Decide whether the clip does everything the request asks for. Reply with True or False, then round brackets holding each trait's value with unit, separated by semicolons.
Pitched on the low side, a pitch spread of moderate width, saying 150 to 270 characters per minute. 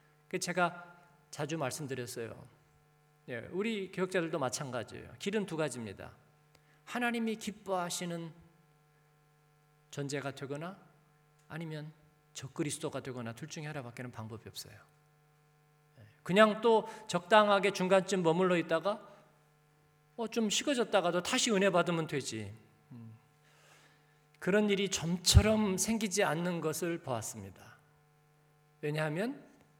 False (150 Hz; 3.7 semitones; 260 characters per minute)